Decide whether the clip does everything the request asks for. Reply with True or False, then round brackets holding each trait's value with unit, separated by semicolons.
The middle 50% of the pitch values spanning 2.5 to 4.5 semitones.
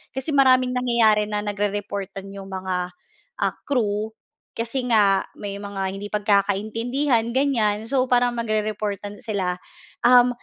True (3.4 semitones)